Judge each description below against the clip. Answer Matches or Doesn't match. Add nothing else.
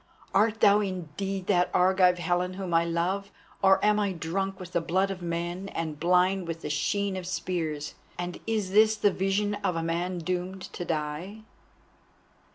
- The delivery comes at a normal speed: Matches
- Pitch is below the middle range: Doesn't match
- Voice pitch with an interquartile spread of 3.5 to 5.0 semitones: Doesn't match